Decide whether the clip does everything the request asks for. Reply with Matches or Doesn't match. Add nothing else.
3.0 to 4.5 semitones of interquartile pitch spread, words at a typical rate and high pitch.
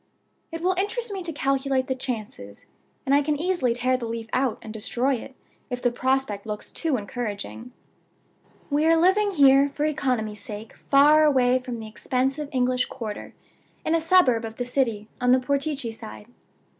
Matches